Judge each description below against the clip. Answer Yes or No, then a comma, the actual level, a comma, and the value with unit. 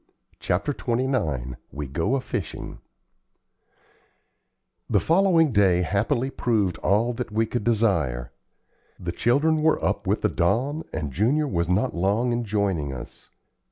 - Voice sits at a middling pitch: No, low, 105 Hz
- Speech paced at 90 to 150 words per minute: Yes, slow, 135 wpm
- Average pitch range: No, wide, 7.0 semitones